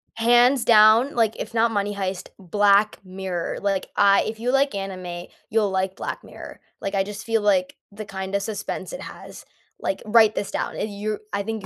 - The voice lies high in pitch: Yes, high, 205 Hz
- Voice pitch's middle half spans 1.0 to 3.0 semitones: Yes, narrow, 2.4 semitones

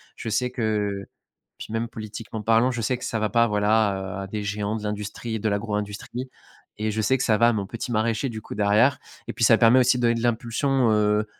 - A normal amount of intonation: No, narrow, 2.0 semitones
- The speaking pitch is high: No, low, 110 Hz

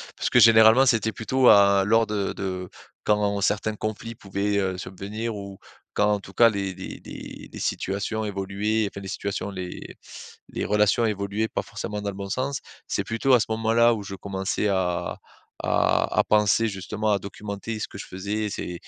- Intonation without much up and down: Yes, narrow, 2.0 semitones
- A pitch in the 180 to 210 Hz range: No, low, 105 Hz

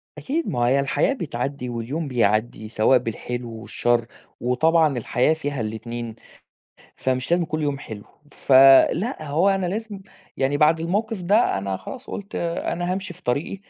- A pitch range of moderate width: No, wide, 6.5 semitones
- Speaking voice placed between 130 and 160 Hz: Yes, medium, 140 Hz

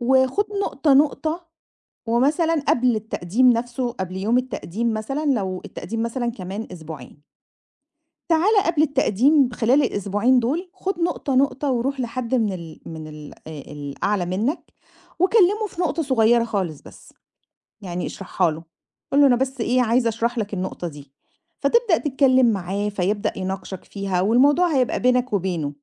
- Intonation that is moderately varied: No, wide, 6.1 semitones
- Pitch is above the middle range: Yes, high, 235 Hz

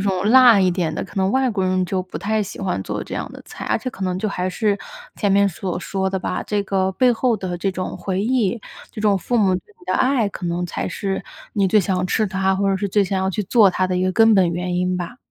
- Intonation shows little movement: Yes, narrow, 2.3 semitones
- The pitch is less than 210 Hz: Yes, high, 195 Hz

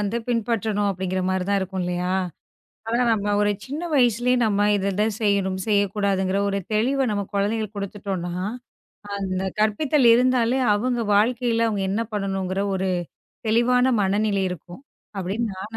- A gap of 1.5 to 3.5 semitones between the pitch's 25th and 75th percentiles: Yes, average, 3.2 semitones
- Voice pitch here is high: Yes, high, 205 Hz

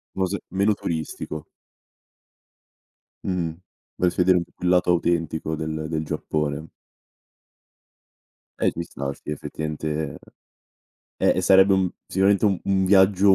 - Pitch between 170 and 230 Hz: No, very low, 90 Hz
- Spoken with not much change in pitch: No, average, 3.4 semitones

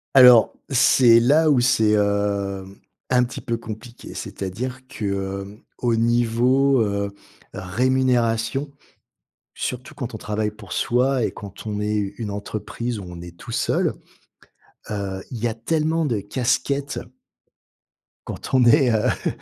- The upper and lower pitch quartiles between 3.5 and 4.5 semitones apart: Yes, average, 3.8 semitones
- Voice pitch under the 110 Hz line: No, low, 115 Hz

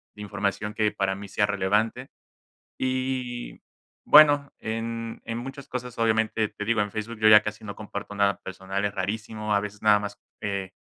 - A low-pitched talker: Yes, low, 105 Hz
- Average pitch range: No, narrow, 2.2 semitones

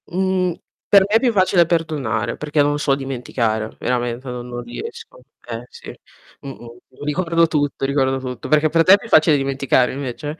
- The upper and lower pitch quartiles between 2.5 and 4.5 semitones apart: No, average, 4.9 semitones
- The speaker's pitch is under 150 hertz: Yes, medium, 140 Hz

